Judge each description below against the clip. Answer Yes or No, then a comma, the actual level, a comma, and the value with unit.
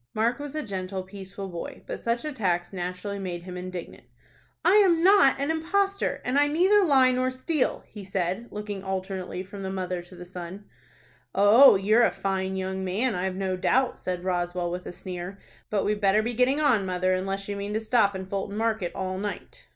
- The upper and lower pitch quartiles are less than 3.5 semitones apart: No, average, 4.7 semitones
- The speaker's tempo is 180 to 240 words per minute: Yes, average, 195 wpm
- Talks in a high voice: Yes, high, 195 Hz